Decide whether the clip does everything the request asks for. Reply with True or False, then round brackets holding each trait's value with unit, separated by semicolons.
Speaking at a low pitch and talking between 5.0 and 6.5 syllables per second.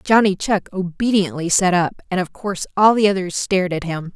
False (190 Hz; 5.5 syllables/s)